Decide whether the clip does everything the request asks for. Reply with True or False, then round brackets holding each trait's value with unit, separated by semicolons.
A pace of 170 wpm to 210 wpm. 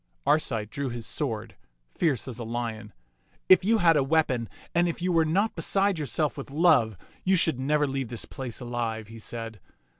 True (185 wpm)